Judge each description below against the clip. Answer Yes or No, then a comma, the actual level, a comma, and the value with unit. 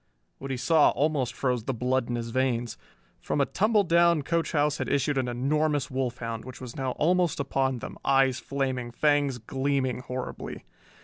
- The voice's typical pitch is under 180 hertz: Yes, low, 135 Hz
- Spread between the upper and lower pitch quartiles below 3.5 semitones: Yes, average, 2.8 semitones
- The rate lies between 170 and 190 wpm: Yes, average, 175 wpm